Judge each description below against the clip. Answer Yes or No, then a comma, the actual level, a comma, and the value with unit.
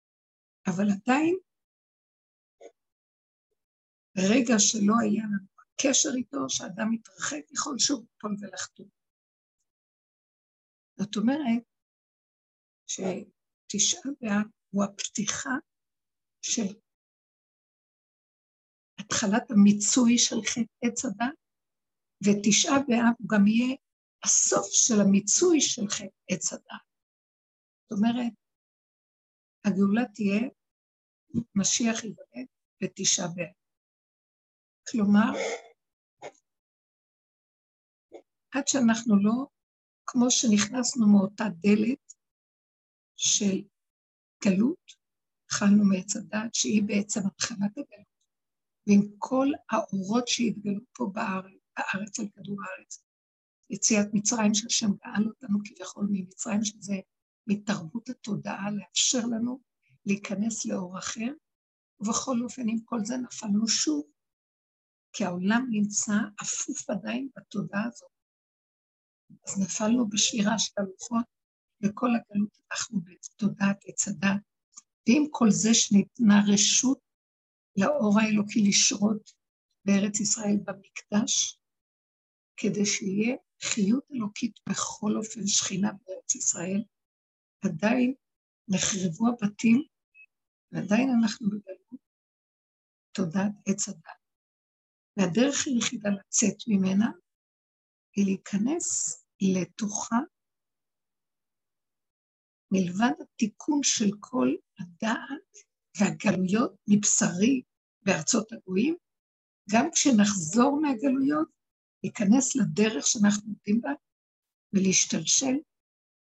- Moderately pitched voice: No, high, 215 Hz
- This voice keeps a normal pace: No, slow, 85 wpm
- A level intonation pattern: No, average, 3.4 semitones